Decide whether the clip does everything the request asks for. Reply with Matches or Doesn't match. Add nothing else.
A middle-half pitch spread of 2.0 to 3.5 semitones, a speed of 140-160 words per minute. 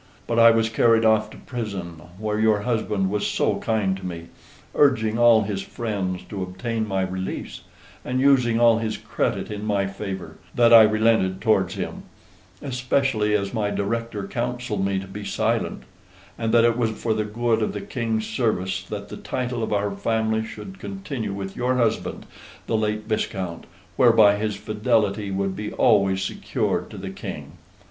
Doesn't match